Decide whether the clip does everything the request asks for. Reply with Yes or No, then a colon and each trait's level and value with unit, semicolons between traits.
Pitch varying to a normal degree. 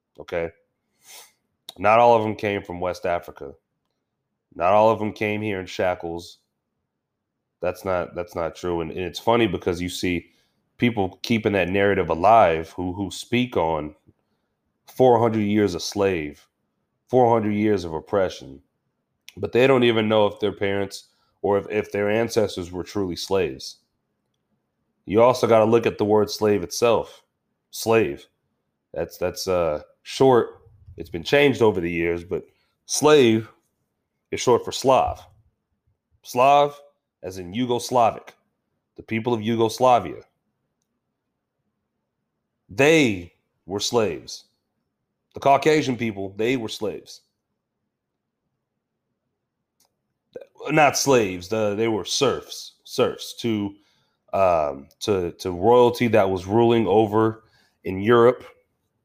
Yes: average, 4.3 semitones